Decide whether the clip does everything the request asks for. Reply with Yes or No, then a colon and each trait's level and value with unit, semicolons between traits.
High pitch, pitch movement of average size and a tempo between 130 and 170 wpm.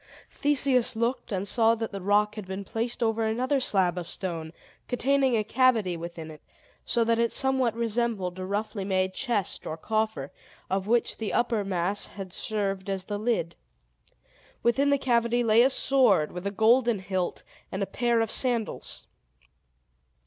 Yes: high, 220 Hz; average, 3.9 semitones; average, 165 wpm